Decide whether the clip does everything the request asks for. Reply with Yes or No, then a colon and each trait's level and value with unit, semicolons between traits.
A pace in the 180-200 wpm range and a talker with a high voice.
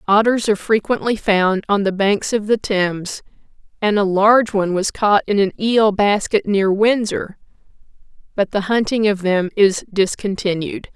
No: average, 160 wpm; high, 205 Hz